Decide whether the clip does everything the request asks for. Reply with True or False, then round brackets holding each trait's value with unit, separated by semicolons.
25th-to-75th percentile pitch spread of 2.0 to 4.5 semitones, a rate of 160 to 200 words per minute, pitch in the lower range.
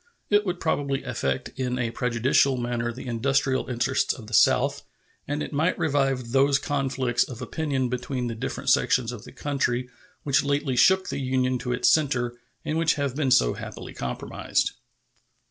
True (2.5 semitones; 170 wpm; 130 Hz)